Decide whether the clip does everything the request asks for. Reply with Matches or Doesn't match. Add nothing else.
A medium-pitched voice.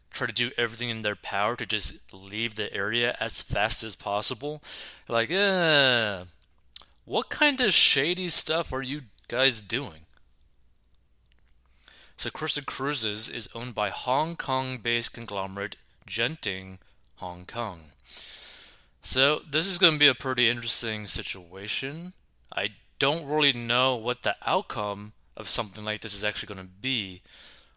Doesn't match